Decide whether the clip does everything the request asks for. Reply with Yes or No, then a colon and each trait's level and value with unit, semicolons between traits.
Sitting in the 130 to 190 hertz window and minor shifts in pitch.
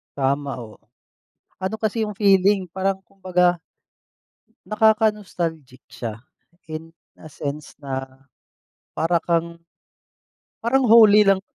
No: medium, 185 Hz; average, 4.9 semitones